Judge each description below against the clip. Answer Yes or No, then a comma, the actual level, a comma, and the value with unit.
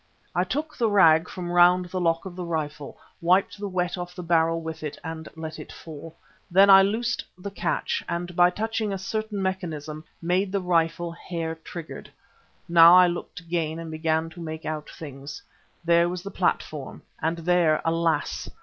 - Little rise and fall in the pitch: Yes, narrow, 2.1 semitones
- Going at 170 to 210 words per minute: Yes, average, 180 wpm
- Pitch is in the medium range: Yes, medium, 170 Hz